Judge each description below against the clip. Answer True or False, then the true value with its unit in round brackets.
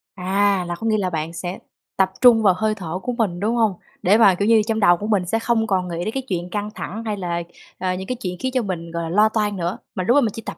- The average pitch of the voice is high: True (200 Hz)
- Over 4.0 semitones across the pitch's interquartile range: False (3.6 semitones)